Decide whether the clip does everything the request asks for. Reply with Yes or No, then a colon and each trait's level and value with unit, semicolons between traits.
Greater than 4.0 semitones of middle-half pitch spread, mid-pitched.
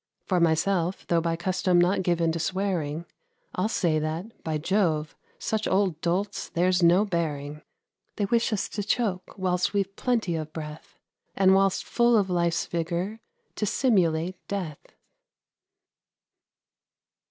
No: average, 3.1 semitones; medium, 180 Hz